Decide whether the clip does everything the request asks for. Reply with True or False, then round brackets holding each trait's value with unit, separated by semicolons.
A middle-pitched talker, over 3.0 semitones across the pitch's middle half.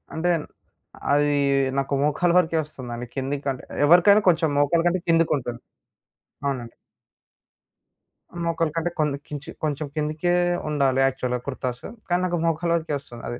True (150 Hz; 3.7 semitones)